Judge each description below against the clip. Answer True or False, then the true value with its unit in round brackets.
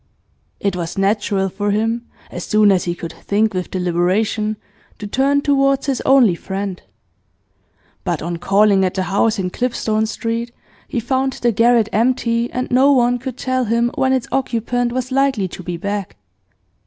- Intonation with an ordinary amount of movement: True (4.4 semitones)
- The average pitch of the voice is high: True (220 Hz)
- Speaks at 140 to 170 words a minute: True (165 wpm)